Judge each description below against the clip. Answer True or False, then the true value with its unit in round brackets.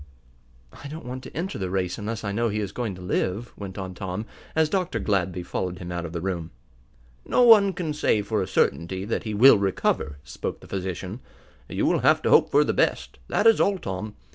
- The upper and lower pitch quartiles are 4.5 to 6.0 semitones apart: True (5.2 semitones)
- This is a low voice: True (100 Hz)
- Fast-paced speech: True (220 wpm)